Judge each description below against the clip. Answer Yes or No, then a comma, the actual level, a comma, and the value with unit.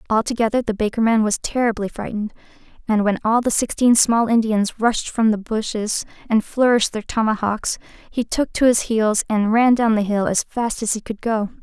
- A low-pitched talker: No, high, 220 Hz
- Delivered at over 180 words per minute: Yes, average, 195 wpm